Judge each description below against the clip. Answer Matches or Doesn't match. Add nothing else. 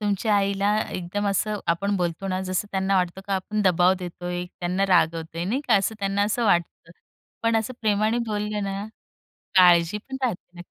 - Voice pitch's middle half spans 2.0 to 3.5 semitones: Matches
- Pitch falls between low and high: Doesn't match